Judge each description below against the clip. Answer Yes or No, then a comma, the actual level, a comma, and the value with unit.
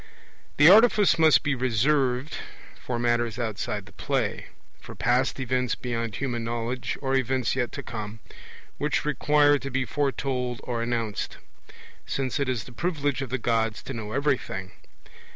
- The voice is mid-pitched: No, low, 125 Hz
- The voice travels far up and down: No, average, 3.1 semitones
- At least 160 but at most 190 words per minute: No, average, 150 wpm